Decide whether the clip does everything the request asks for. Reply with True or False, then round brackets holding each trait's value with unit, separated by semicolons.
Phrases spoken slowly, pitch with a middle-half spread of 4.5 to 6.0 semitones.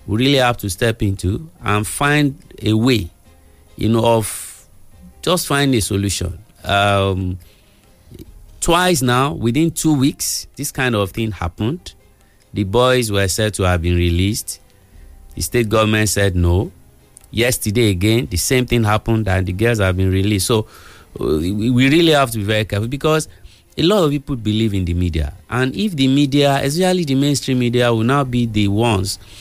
False (170 wpm; 5.0 semitones)